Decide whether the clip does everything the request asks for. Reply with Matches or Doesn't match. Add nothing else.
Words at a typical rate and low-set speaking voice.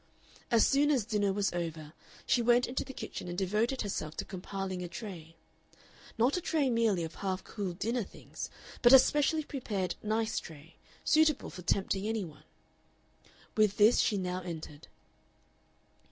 Doesn't match